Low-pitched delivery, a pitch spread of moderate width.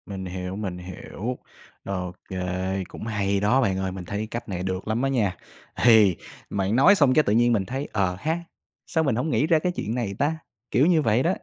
No: low, 105 Hz; wide, 5.7 semitones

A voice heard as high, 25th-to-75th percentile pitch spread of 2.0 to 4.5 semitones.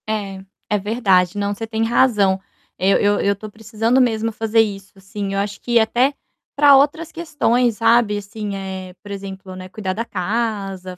Yes: high, 210 Hz; average, 2.8 semitones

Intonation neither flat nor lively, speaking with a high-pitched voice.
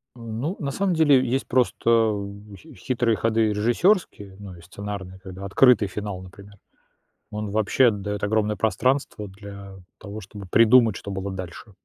No: average, 3.4 semitones; low, 105 Hz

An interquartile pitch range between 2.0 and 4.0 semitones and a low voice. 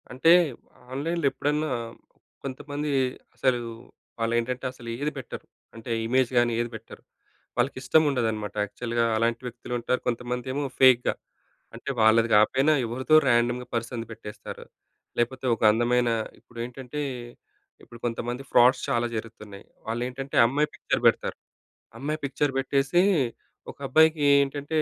Yes: average, 2.7 semitones; low, 125 Hz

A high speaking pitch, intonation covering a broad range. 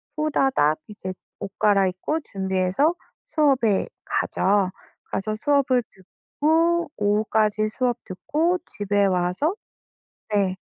Yes: high, 215 Hz; wide, 7.2 semitones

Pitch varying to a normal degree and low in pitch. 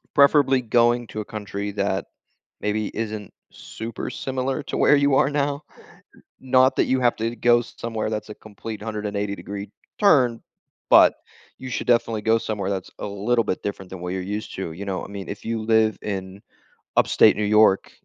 Yes: average, 3.0 semitones; low, 110 Hz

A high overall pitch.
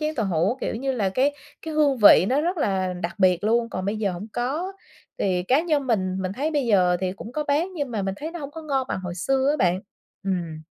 Yes: high, 230 Hz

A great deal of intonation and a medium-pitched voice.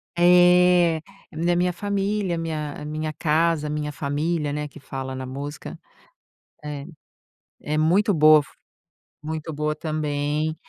No: narrow, 2.6 semitones; medium, 155 Hz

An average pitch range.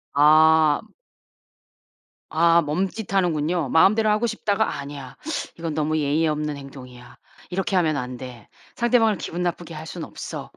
Yes: average, 3.8 semitones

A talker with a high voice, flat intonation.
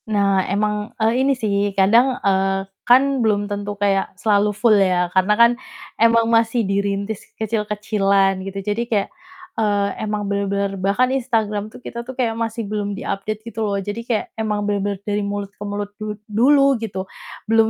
Yes: high, 210 Hz; narrow, 2.1 semitones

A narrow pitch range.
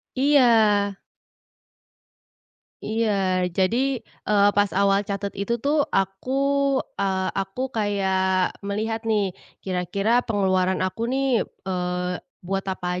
No: average, 3.0 semitones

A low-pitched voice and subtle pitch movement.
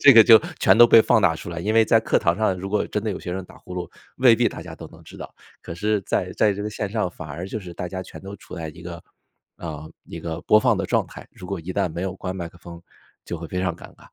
No: very low, 95 Hz; average, 3.7 semitones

